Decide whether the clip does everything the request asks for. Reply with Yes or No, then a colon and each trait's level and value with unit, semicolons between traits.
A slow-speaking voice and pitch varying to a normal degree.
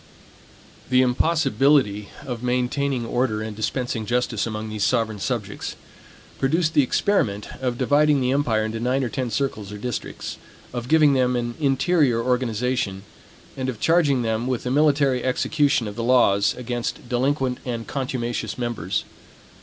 No: average, 145 wpm; average, 3.1 semitones